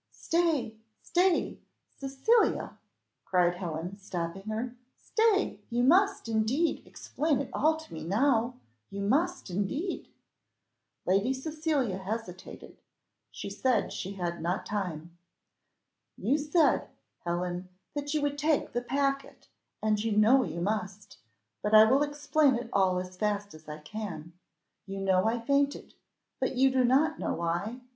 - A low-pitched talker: No, high, 225 Hz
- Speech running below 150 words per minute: Yes, slow, 135 wpm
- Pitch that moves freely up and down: Yes, wide, 7.2 semitones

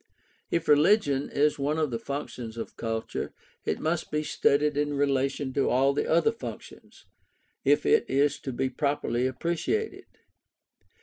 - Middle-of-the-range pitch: Yes, medium, 145 Hz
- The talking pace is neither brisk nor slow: Yes, average, 145 wpm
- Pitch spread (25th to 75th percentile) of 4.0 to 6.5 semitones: No, average, 2.7 semitones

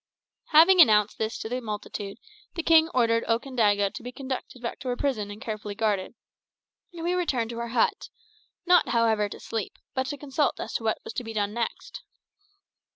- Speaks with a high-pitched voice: Yes, high, 235 Hz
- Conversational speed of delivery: Yes, average, 190 wpm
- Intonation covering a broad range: No, average, 4.0 semitones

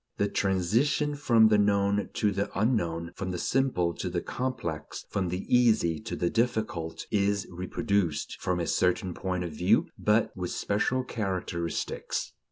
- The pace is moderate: Yes, average, 155 wpm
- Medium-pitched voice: No, low, 100 Hz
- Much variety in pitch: No, average, 4.0 semitones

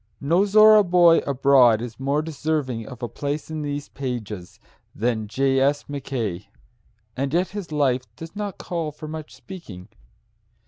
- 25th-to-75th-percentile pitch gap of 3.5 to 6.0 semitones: Yes, average, 4.7 semitones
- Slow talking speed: No, average, 150 wpm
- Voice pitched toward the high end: No, medium, 140 Hz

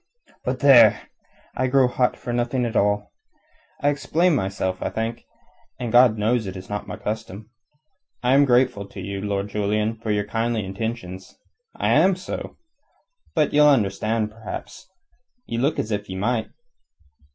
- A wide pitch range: No, average, 3.4 semitones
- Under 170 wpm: Yes, average, 160 wpm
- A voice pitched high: No, low, 110 Hz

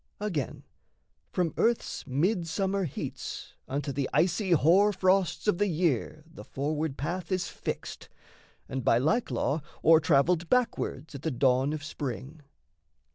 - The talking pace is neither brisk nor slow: No, slow, 130 wpm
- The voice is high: No, medium, 160 Hz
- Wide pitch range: No, average, 4.8 semitones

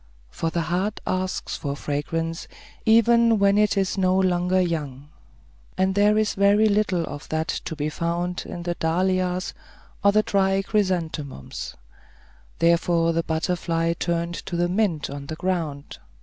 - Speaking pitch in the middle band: Yes, medium, 175 Hz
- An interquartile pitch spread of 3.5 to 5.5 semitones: No, average, 2.9 semitones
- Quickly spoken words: No, average, 150 wpm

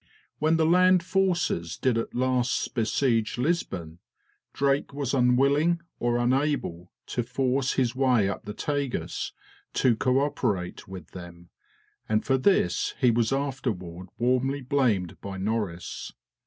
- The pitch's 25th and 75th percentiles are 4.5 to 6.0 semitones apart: Yes, average, 5.1 semitones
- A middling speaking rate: No, slow, 130 wpm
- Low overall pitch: Yes, low, 125 Hz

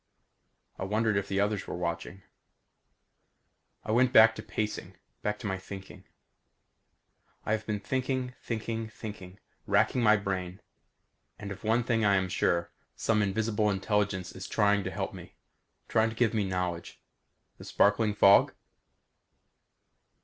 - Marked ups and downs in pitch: No, average, 2.7 semitones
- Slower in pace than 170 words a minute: Yes, average, 140 wpm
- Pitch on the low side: Yes, low, 105 Hz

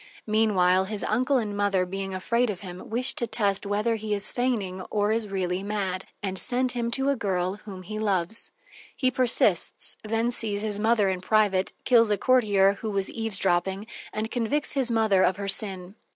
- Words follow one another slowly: No, average, 185 wpm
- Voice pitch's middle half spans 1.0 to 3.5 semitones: Yes, average, 3.0 semitones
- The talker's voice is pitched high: Yes, high, 210 Hz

